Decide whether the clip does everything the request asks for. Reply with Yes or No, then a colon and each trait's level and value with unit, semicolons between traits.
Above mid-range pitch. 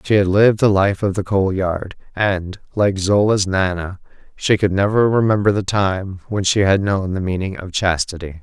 No: very low, 95 Hz